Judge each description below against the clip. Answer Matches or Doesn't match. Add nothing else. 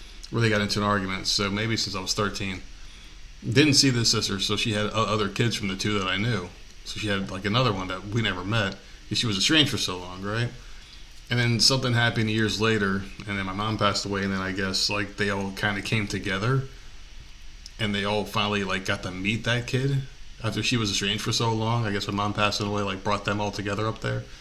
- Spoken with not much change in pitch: Matches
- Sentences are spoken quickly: Matches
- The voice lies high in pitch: Doesn't match